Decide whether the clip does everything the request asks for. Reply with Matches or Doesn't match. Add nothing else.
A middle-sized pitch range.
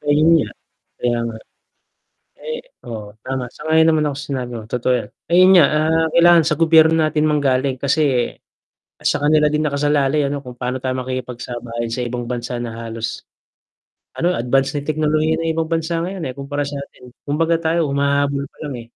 Matches